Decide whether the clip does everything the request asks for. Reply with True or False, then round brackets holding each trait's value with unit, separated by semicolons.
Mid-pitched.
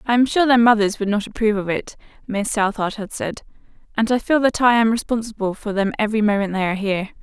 False (215 Hz)